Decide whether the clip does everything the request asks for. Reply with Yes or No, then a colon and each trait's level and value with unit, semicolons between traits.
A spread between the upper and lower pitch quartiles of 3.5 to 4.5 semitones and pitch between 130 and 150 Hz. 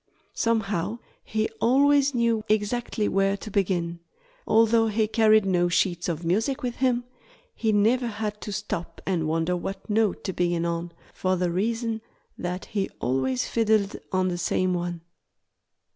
No: average, 4.2 semitones; high, 205 Hz